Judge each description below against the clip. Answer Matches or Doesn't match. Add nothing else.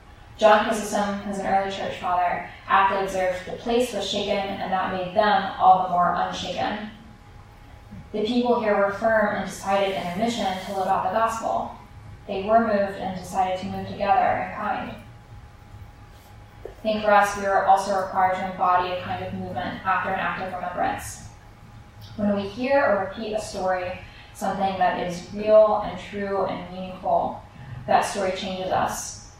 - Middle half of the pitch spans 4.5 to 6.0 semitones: Doesn't match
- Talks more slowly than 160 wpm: Doesn't match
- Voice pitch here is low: Doesn't match